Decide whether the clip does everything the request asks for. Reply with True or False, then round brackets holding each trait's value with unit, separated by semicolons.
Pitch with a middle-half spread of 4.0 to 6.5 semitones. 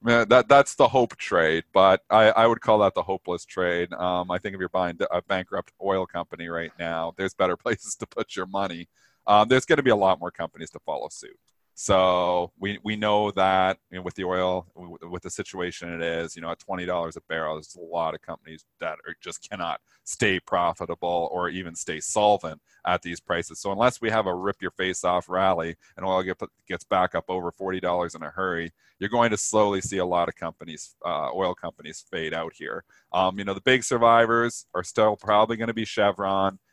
False (3.1 semitones)